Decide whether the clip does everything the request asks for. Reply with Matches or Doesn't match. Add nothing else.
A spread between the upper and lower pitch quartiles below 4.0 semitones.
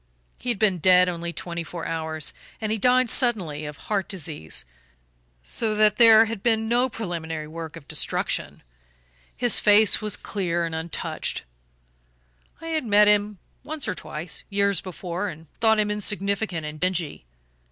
Doesn't match